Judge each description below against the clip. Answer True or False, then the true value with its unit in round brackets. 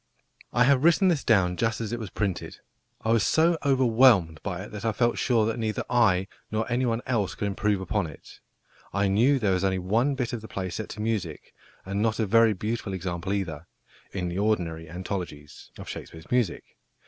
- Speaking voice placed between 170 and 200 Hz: False (105 Hz)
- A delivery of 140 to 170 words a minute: False (200 wpm)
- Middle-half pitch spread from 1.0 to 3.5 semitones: False (4.0 semitones)